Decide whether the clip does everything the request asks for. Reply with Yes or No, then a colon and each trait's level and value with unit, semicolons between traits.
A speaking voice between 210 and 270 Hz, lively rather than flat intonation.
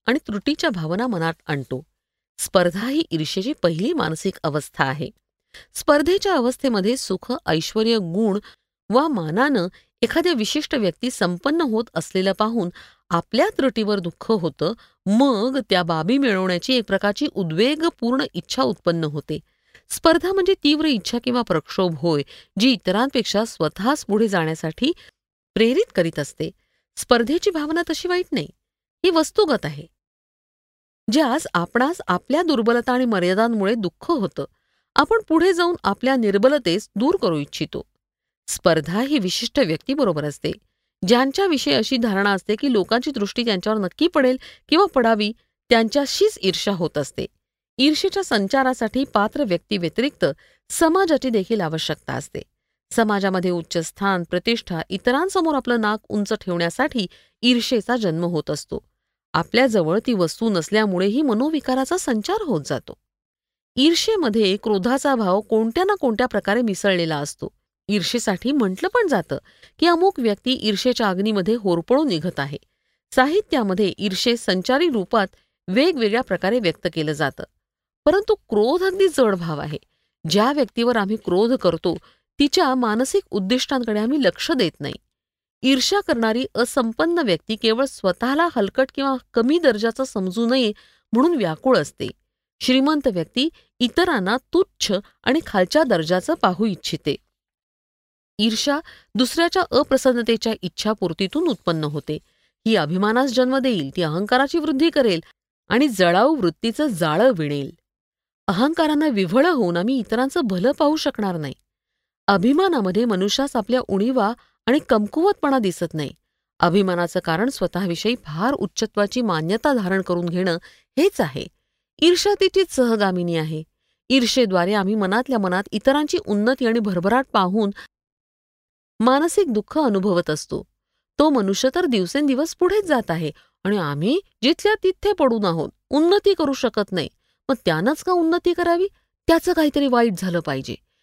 Yes: high, 230 Hz; wide, 6.7 semitones